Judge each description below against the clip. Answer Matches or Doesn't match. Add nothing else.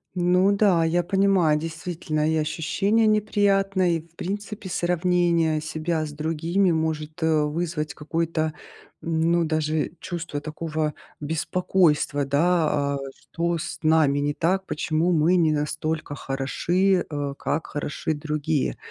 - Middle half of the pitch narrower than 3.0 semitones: Matches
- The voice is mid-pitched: Matches